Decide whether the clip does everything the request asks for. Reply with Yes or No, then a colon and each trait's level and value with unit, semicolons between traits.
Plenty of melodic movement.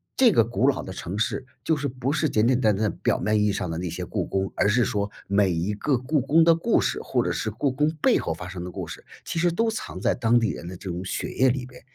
Yes: wide, 6.0 semitones